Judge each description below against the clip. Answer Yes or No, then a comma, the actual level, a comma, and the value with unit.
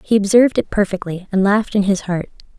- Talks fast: Yes, fast, 210 wpm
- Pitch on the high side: Yes, high, 200 Hz